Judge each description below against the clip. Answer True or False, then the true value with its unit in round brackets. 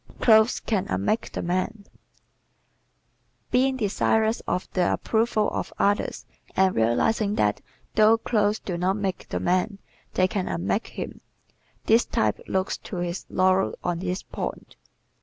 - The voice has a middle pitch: False (195 Hz)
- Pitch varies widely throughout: False (3.4 semitones)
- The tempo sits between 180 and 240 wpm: False (140 wpm)